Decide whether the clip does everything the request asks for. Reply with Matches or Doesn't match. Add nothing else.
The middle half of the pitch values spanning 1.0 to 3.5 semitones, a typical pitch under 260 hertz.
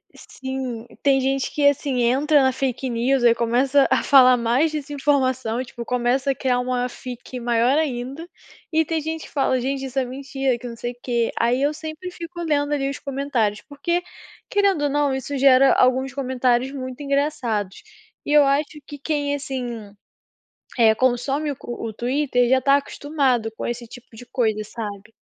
Doesn't match